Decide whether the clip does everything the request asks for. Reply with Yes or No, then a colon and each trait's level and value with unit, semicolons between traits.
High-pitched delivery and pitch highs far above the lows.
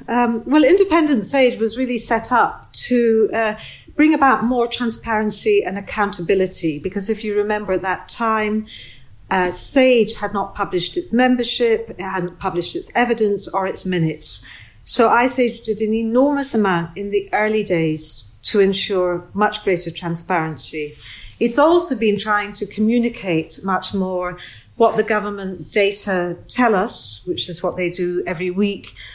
No: high, 205 Hz; average, 4.3 semitones